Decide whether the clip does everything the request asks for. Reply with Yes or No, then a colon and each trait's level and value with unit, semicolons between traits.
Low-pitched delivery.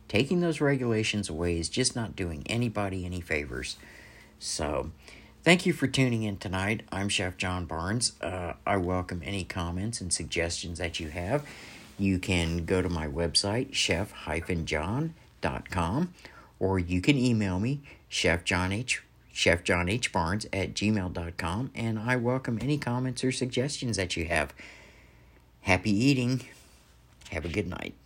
Yes: very low, 95 Hz